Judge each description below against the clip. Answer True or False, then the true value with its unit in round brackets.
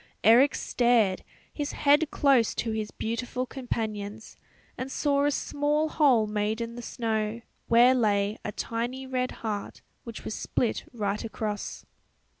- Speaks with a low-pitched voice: False (235 Hz)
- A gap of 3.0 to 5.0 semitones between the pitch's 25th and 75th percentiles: True (3.3 semitones)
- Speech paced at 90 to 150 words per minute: True (140 wpm)